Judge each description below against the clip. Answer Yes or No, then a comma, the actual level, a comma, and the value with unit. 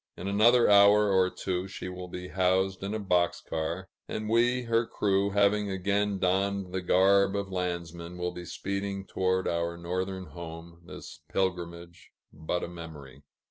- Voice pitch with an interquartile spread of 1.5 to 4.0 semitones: Yes, narrow, 2.4 semitones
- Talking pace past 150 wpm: Yes, average, 160 wpm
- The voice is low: Yes, very low, 95 Hz